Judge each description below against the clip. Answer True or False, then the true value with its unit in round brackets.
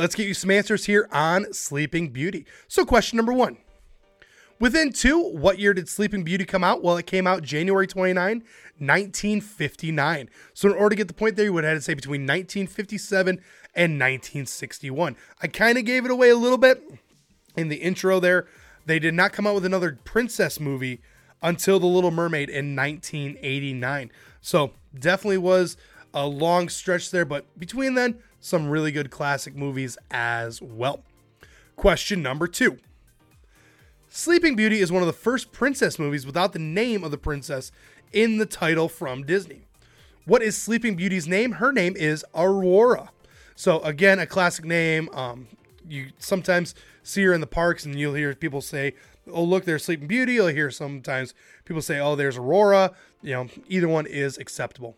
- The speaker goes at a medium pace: True (175 wpm)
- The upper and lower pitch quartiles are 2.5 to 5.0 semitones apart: False (5.5 semitones)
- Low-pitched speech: False (175 Hz)